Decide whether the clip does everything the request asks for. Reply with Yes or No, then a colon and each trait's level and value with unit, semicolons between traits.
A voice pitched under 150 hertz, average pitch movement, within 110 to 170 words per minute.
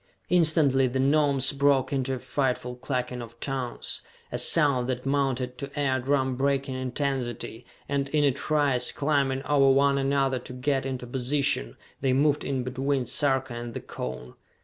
No: low, 135 Hz; narrow, 1.8 semitones; average, 160 wpm